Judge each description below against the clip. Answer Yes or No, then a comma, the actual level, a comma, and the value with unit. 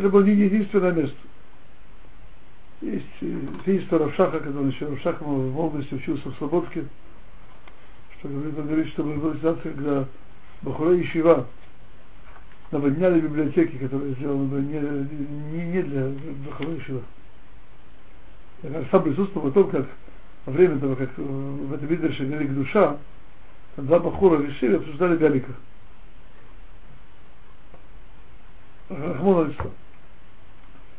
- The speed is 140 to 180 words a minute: No, slow, 110 wpm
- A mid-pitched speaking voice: Yes, medium, 150 Hz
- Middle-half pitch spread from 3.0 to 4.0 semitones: Yes, average, 3.3 semitones